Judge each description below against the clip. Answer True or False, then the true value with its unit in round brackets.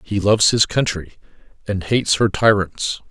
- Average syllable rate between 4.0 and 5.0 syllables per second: True (4.9 syllables/s)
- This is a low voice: True (100 Hz)